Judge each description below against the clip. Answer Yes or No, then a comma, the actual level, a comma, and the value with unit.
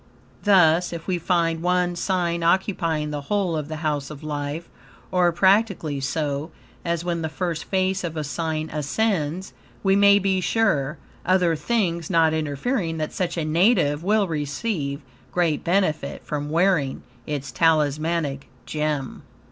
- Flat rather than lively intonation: No, average, 3.4 semitones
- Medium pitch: Yes, medium, 165 Hz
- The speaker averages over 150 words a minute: No, average, 145 wpm